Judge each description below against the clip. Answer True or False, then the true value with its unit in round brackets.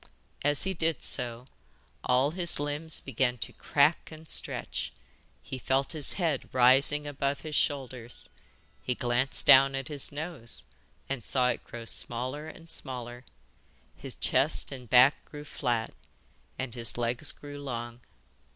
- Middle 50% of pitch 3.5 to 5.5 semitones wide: False (3.1 semitones)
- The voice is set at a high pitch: False (135 Hz)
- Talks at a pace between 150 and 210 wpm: False (140 wpm)